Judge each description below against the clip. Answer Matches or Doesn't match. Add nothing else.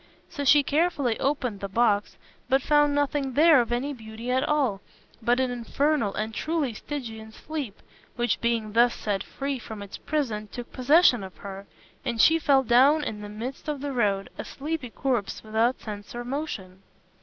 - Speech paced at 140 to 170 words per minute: Doesn't match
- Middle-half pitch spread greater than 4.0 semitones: Matches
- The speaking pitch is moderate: Doesn't match